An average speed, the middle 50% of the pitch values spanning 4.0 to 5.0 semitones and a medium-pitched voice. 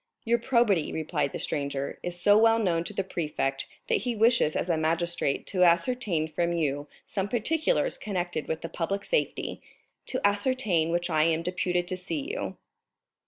Yes: average, 170 wpm; average, 4.7 semitones; medium, 175 Hz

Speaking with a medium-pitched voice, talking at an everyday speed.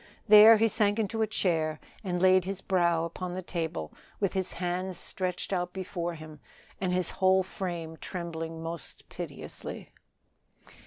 Yes: medium, 180 Hz; average, 150 wpm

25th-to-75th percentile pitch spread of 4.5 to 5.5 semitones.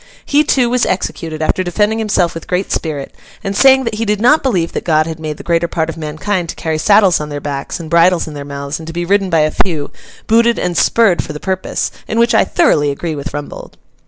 Yes: average, 5.0 semitones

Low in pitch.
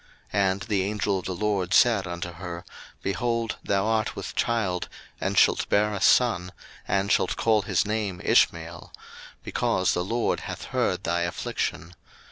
Yes: very low, 95 Hz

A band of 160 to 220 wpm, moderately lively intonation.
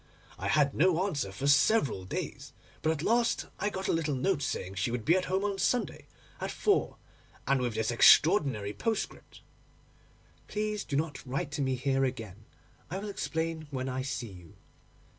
No: average, 180 wpm; wide, 6.9 semitones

